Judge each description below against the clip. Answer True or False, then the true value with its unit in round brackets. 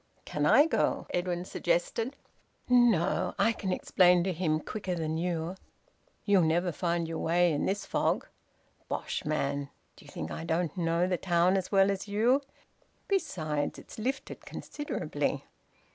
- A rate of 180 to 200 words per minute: False (145 wpm)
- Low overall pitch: False (175 Hz)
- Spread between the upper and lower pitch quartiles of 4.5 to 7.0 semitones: False (3.5 semitones)